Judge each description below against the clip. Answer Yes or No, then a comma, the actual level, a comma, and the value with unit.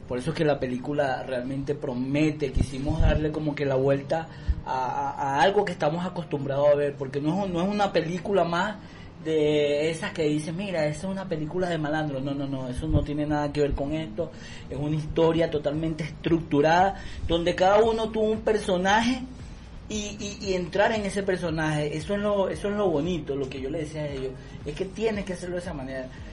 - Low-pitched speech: No, medium, 155 Hz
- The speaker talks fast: Yes, fast, 210 wpm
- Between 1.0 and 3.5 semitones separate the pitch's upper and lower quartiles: No, average, 4.7 semitones